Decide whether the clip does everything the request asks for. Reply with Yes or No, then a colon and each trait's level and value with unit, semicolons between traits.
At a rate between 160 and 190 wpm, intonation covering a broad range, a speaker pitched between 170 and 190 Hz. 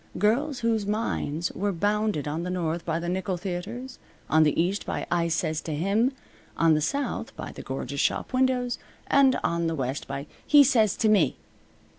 Yes: average, 185 wpm; wide, 6.0 semitones; medium, 185 Hz